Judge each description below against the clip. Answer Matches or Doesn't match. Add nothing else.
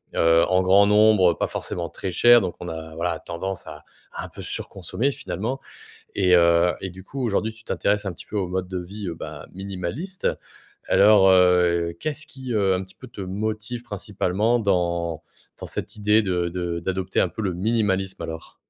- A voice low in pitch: Matches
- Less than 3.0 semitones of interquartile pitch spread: Doesn't match